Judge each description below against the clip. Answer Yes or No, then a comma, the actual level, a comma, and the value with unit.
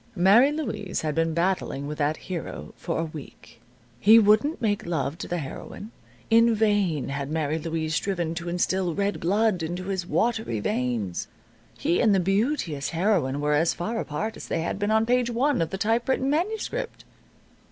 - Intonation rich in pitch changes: Yes, wide, 5.7 semitones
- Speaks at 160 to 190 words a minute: Yes, average, 175 wpm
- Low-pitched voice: No, medium, 185 Hz